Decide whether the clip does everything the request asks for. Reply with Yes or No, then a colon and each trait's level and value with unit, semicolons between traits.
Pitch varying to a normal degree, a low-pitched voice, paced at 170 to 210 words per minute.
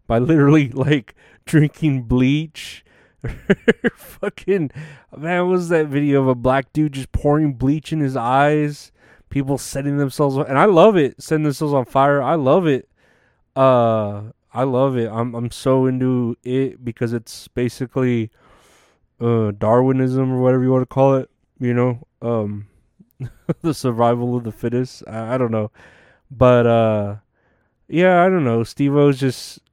No: average, 3.3 semitones; low, 130 Hz; average, 155 wpm